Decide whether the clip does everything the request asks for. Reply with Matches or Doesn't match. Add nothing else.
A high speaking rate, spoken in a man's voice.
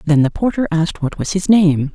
Doesn't match